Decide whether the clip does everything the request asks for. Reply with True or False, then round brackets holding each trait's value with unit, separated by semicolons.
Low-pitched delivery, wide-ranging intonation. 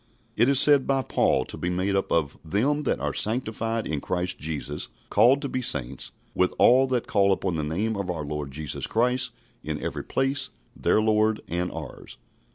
True (105 Hz; 6.9 semitones)